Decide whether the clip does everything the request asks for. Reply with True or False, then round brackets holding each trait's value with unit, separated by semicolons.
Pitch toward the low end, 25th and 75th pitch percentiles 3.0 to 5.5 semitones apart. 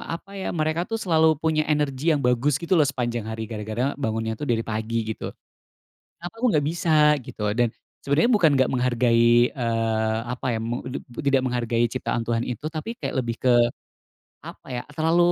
True (125 Hz; 5.0 semitones)